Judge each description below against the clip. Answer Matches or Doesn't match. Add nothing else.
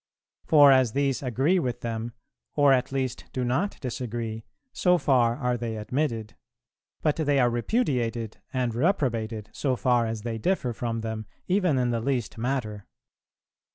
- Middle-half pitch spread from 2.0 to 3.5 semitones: Matches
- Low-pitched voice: Matches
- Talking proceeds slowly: Doesn't match